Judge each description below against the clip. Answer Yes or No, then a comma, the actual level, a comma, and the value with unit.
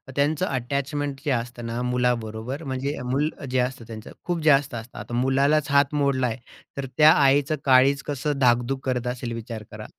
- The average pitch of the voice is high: No, low, 130 Hz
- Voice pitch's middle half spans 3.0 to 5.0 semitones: No, narrow, 2.6 semitones